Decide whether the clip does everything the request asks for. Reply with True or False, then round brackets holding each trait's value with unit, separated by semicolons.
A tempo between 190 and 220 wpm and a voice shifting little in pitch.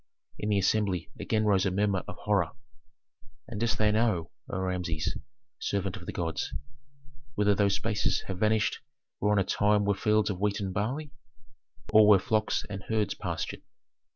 False (170 wpm; 2.1 semitones)